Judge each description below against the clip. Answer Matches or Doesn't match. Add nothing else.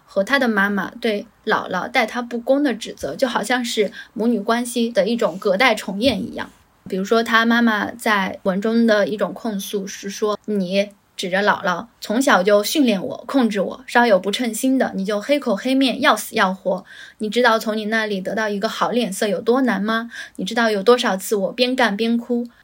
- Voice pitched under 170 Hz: Doesn't match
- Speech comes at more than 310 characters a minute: Doesn't match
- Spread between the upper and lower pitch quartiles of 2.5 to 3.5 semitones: Matches